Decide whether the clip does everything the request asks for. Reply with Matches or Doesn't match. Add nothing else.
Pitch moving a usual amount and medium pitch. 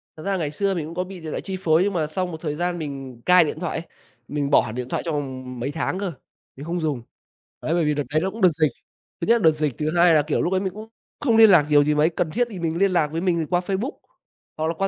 Matches